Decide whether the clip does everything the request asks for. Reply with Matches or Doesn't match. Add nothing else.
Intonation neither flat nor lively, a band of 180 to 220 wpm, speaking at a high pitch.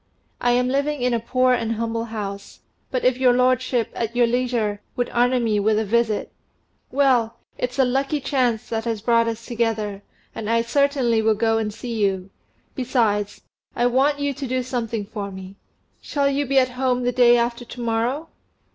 Doesn't match